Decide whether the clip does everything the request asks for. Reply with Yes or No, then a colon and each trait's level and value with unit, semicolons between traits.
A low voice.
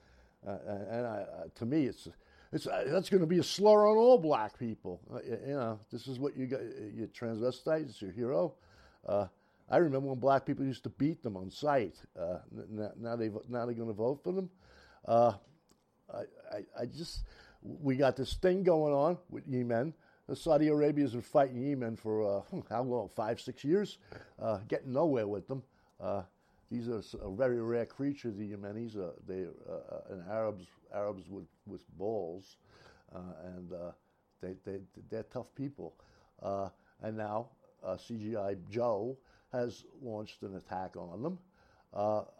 Yes: low, 115 Hz